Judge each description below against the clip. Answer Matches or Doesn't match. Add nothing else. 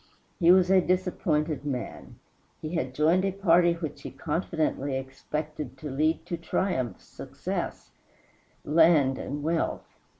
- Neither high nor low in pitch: Matches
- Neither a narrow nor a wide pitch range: Matches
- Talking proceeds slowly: Matches